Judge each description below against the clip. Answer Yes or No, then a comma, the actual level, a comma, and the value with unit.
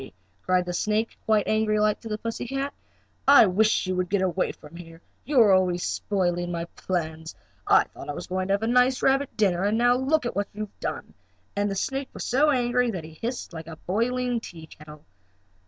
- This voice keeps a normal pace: No, fast, 215 wpm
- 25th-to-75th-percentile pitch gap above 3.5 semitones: Yes, wide, 5.4 semitones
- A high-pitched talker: Yes, high, 205 Hz